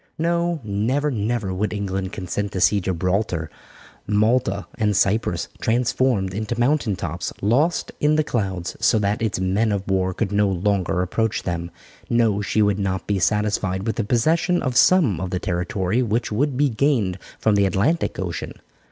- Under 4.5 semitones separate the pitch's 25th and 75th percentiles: Yes, average, 4.0 semitones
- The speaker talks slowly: No, average, 170 wpm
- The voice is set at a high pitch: No, low, 105 Hz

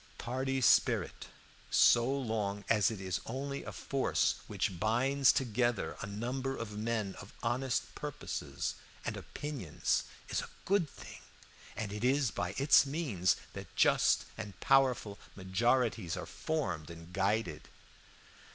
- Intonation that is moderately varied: Yes, average, 5.0 semitones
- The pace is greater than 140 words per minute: No, slow, 135 wpm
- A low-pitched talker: Yes, low, 115 Hz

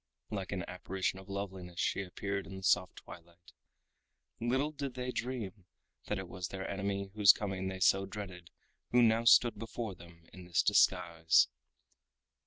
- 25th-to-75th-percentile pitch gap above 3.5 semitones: No, average, 2.9 semitones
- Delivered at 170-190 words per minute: No, average, 160 wpm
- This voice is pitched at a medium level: No, very low, 95 Hz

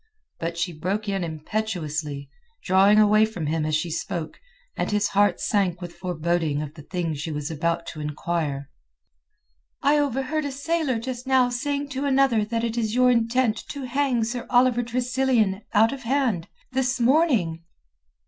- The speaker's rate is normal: Yes, average, 160 wpm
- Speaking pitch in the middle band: No, high, 215 Hz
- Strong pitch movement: Yes, wide, 7.2 semitones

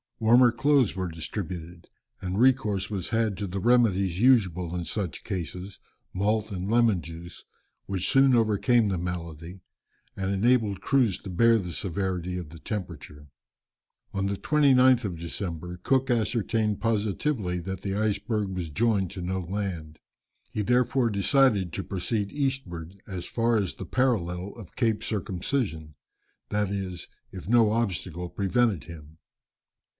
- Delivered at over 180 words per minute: No, average, 145 wpm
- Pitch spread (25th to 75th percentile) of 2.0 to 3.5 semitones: No, average, 4.4 semitones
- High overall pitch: No, low, 100 Hz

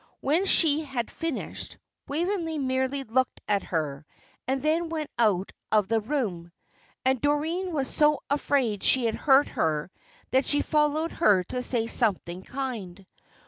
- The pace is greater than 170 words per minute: No, average, 145 wpm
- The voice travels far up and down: Yes, wide, 5.9 semitones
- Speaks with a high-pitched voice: Yes, very high, 265 Hz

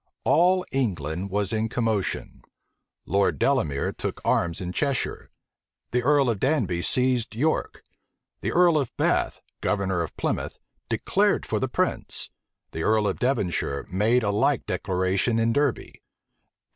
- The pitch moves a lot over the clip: Yes, wide, 6.0 semitones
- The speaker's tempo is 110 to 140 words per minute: Yes, slow, 135 wpm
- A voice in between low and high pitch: No, low, 110 Hz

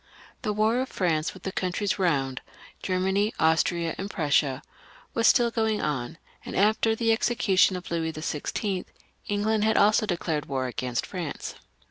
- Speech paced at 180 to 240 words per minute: No, average, 165 wpm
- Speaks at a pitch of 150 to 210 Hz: Yes, medium, 185 Hz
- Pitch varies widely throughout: No, average, 5.0 semitones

